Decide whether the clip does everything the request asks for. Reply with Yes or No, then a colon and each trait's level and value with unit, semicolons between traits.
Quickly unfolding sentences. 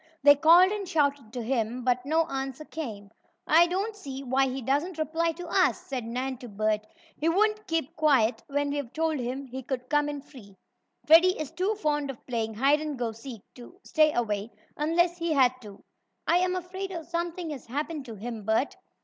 No: average, 195 wpm